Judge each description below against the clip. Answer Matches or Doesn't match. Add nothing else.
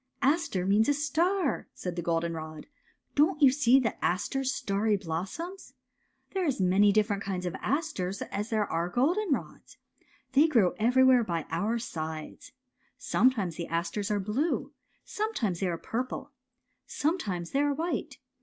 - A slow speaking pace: Doesn't match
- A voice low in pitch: Doesn't match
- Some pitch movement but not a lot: Doesn't match